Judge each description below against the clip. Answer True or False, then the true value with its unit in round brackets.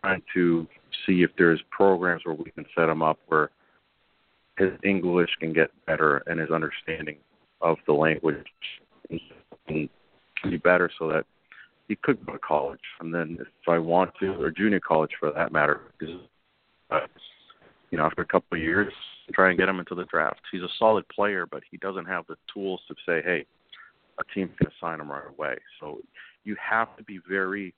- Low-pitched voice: True (90 Hz)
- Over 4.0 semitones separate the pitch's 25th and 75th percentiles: False (2.9 semitones)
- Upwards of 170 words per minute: True (190 wpm)